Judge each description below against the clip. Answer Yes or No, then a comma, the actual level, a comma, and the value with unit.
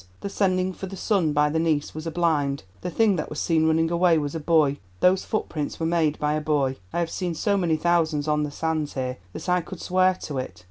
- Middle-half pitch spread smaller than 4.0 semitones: Yes, average, 3.1 semitones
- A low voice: No, medium, 160 Hz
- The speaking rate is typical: No, fast, 240 wpm